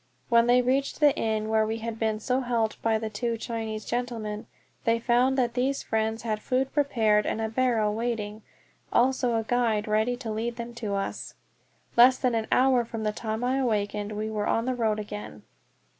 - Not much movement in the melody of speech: Yes, narrow, 2.2 semitones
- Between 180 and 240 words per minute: Yes, average, 195 wpm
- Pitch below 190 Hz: No, high, 230 Hz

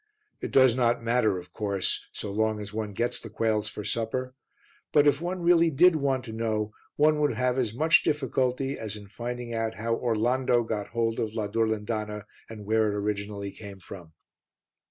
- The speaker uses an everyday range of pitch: Yes, average, 3.3 semitones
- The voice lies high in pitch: No, low, 115 Hz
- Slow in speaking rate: No, average, 185 wpm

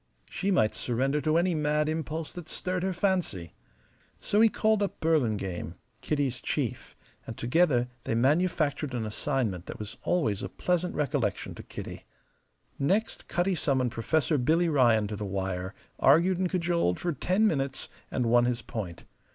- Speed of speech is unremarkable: Yes, average, 160 wpm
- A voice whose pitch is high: No, medium, 145 Hz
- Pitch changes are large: Yes, wide, 7.2 semitones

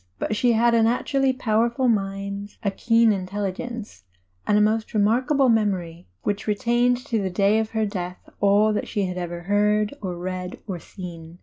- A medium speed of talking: Yes, average, 185 wpm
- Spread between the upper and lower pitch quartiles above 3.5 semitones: No, average, 3.2 semitones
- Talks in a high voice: Yes, high, 210 Hz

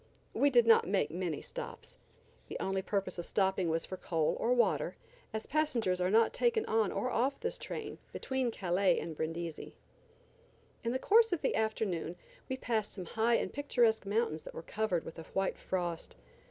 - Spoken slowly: No, average, 180 wpm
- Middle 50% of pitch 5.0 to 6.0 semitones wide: Yes, wide, 5.6 semitones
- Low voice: No, high, 215 Hz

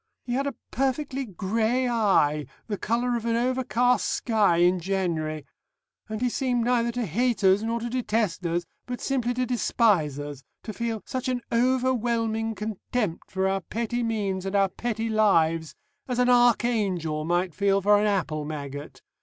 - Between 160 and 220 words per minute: Yes, average, 165 wpm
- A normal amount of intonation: Yes, average, 4.5 semitones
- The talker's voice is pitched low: No, high, 220 Hz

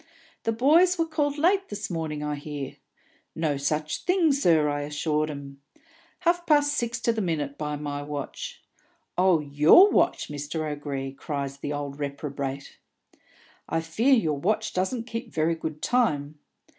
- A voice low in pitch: No, medium, 155 Hz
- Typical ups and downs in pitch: No, wide, 8.4 semitones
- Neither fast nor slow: Yes, average, 155 wpm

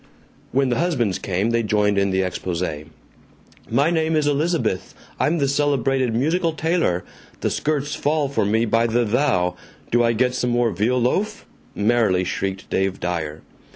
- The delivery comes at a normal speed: Yes, average, 160 wpm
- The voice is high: No, low, 120 Hz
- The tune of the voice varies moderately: No, wide, 6.8 semitones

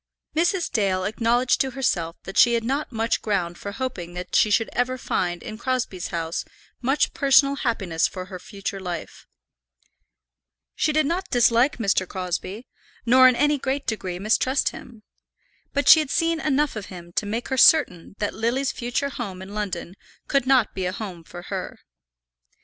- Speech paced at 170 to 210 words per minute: Yes, average, 180 wpm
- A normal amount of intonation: No, wide, 6.1 semitones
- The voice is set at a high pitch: Yes, high, 230 Hz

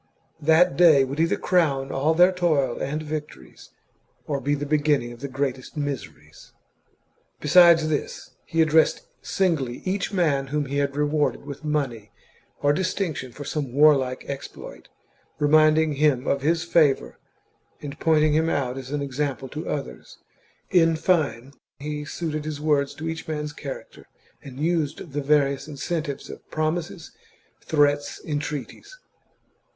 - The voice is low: No, medium, 150 Hz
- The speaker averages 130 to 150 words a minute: Yes, average, 140 wpm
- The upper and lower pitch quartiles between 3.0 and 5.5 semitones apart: No, narrow, 2.4 semitones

